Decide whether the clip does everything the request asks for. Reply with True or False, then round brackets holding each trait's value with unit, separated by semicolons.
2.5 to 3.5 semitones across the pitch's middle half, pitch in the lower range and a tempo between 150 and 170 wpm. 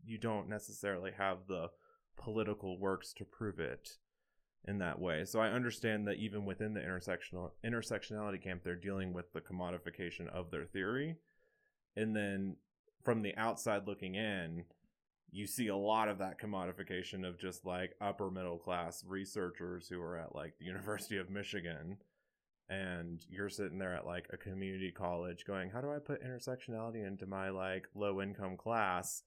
True (2.9 semitones; 100 Hz; 165 wpm)